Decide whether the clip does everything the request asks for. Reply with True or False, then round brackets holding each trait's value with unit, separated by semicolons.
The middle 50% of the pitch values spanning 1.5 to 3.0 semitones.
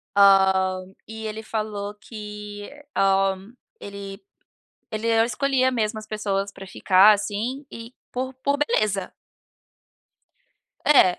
True (2.5 semitones)